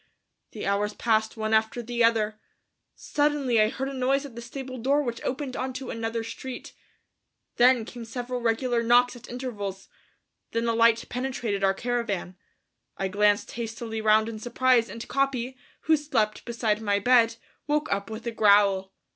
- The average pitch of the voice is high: Yes, high, 230 Hz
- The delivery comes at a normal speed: Yes, average, 165 wpm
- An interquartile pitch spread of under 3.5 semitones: Yes, average, 2.7 semitones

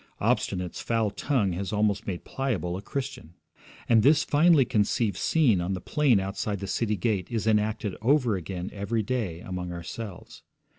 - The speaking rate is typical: Yes, average, 160 wpm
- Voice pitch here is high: No, low, 105 Hz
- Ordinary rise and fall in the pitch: Yes, average, 4.0 semitones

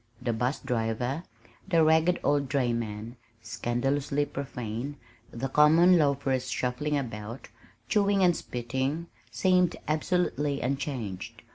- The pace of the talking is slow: Yes, slow, 110 wpm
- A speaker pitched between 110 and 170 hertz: Yes, medium, 140 Hz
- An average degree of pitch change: Yes, average, 4.2 semitones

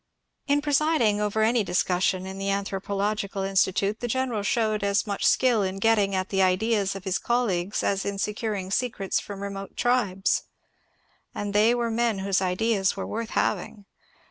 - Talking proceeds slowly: No, average, 170 wpm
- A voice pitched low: No, high, 200 Hz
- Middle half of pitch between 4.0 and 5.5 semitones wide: No, narrow, 2.6 semitones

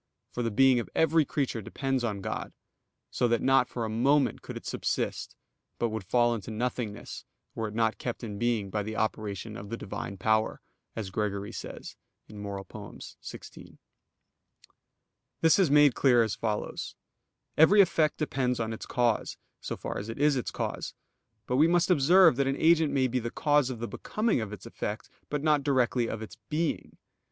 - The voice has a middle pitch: No, low, 120 Hz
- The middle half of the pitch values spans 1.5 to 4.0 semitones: No, average, 4.5 semitones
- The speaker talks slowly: No, average, 180 wpm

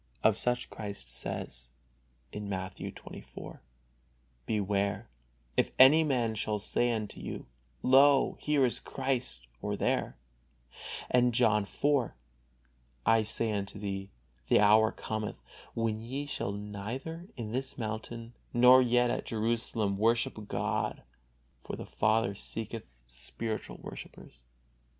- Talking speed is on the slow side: Yes, slow, 120 wpm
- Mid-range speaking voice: No, low, 110 Hz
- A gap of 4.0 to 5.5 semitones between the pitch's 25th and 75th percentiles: No, average, 3.0 semitones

